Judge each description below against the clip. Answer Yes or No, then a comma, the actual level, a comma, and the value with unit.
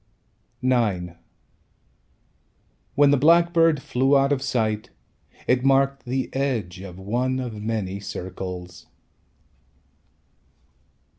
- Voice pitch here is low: Yes, low, 125 Hz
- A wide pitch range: Yes, wide, 5.7 semitones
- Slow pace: Yes, slow, 90 wpm